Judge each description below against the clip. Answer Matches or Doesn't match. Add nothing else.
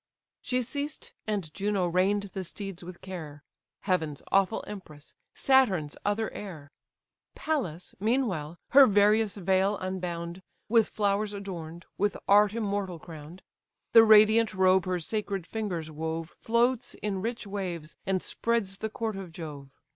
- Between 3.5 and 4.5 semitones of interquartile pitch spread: Matches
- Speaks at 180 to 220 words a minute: Doesn't match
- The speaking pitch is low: Doesn't match